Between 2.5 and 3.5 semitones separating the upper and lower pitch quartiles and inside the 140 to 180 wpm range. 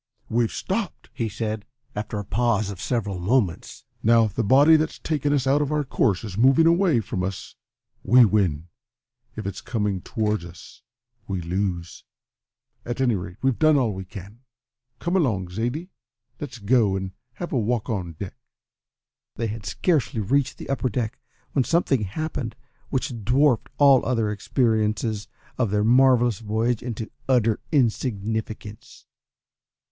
No: average, 4.4 semitones; average, 155 wpm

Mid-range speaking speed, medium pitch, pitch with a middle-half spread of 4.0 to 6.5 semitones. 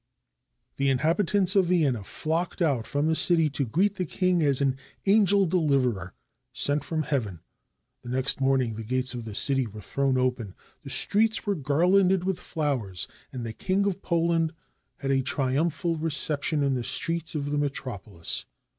Yes: average, 170 wpm; medium, 145 Hz; average, 5.0 semitones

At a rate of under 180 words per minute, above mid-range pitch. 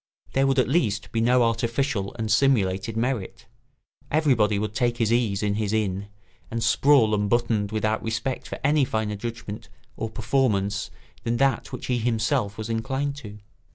No: average, 160 wpm; low, 115 Hz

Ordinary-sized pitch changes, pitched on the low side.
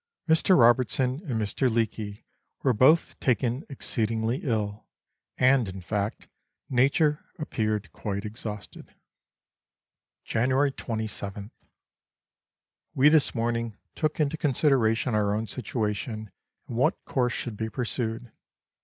Yes: average, 3.5 semitones; low, 115 Hz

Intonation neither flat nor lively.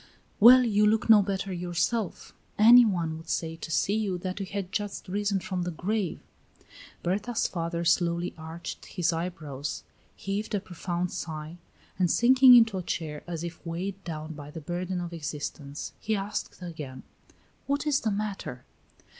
Yes: average, 3.9 semitones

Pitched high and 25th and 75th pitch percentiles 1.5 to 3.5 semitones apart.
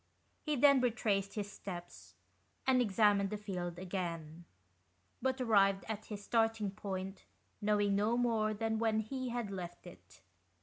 Yes: high, 205 Hz; average, 2.9 semitones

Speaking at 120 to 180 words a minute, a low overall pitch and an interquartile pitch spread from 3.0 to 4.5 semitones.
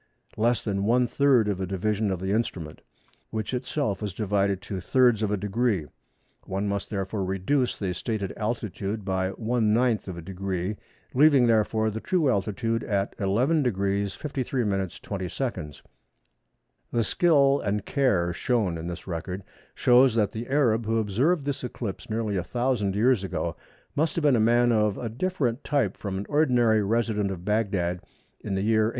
Yes: average, 170 wpm; low, 110 Hz; average, 3.9 semitones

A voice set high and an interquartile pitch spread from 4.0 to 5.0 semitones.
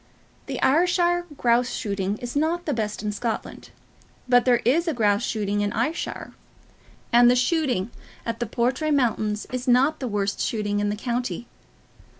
Yes: high, 240 Hz; average, 4.4 semitones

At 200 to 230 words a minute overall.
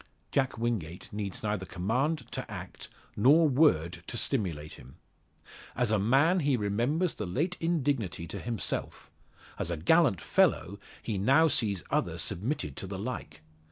No: average, 150 wpm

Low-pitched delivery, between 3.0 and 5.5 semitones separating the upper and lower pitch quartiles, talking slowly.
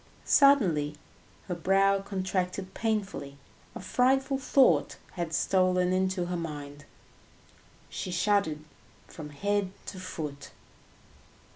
No: medium, 185 Hz; average, 3.7 semitones; slow, 100 wpm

